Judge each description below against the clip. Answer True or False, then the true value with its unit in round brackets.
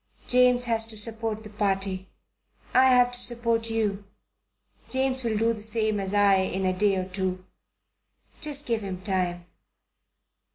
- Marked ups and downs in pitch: False (3.5 semitones)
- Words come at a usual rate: True (155 wpm)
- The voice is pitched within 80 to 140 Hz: False (215 Hz)